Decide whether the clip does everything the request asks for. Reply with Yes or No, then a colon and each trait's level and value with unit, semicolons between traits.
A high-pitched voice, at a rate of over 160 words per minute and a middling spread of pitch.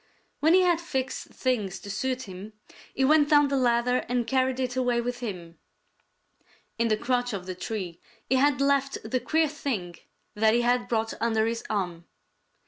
Yes: high, 245 Hz; average, 180 wpm; average, 3.5 semitones